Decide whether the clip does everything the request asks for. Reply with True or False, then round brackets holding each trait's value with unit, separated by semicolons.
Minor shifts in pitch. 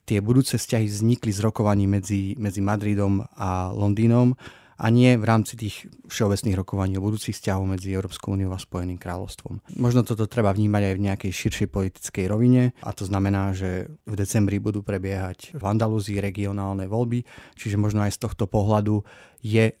True (2.3 semitones)